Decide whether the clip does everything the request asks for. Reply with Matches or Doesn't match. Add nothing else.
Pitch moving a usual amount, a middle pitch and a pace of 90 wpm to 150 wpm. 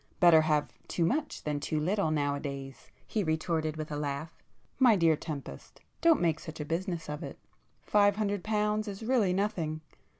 Doesn't match